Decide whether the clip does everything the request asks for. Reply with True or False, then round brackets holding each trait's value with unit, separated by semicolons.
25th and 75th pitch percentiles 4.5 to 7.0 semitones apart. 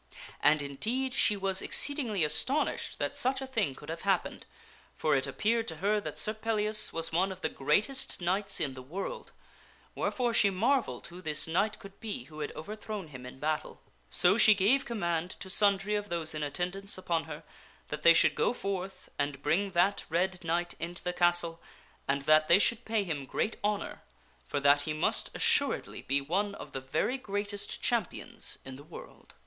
True (5.2 semitones)